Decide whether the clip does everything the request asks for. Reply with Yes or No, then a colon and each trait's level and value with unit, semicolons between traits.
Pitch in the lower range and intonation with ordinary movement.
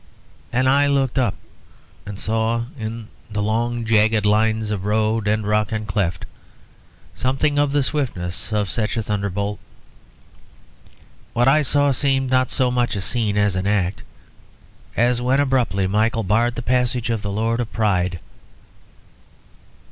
Yes: low, 110 Hz; average, 3.2 semitones